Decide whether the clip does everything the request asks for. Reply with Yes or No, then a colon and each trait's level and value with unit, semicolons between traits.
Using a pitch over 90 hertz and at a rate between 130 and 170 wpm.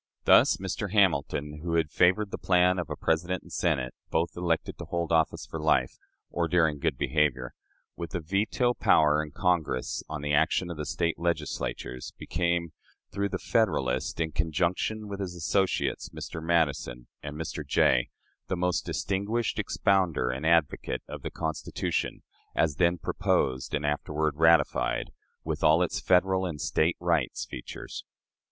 No: very low, 80 Hz; average, 155 wpm